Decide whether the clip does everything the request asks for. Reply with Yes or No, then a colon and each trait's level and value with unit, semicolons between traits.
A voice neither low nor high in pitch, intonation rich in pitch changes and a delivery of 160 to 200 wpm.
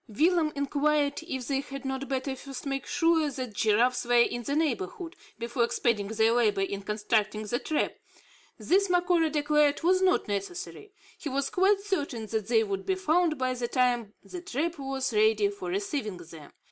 No: very high, 265 Hz; wide, 5.9 semitones; average, 175 wpm